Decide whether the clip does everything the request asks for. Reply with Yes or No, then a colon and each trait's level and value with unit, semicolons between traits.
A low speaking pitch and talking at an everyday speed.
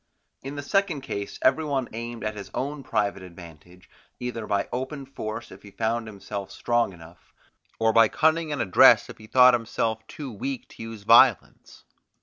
Yes: low, 115 Hz; average, 175 wpm